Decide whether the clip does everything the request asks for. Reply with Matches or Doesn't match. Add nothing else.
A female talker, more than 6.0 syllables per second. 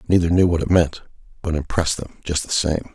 Doesn't match